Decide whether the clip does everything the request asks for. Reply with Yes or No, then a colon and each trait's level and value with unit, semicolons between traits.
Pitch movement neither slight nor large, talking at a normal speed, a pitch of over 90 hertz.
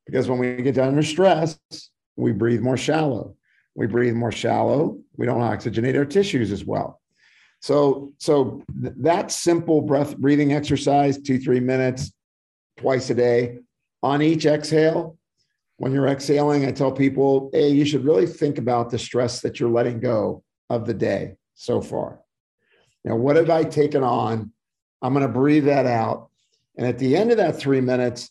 Yes: average, 3.3 semitones; average, 175 wpm; low, 135 Hz